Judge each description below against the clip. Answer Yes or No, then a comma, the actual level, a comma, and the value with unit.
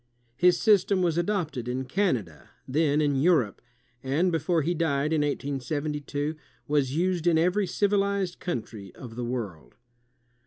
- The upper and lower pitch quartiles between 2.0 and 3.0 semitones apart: No, average, 5.2 semitones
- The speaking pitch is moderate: Yes, medium, 155 Hz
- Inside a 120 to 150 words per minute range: Yes, average, 145 wpm